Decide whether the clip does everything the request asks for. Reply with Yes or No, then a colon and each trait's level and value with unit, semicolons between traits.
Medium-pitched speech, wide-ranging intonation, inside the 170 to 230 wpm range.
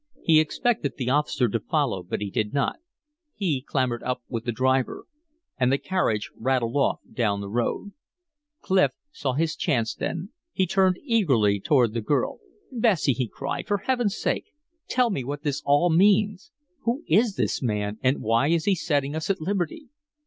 Yes: medium, 145 Hz; wide, 7.6 semitones; average, 175 wpm